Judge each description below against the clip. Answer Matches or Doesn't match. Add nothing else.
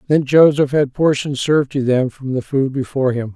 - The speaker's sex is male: Matches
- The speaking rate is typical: Doesn't match